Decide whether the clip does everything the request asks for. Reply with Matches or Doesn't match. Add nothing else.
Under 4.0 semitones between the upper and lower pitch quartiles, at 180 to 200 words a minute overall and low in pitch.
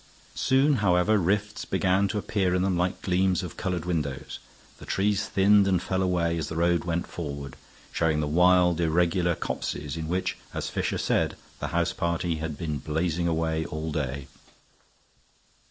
Doesn't match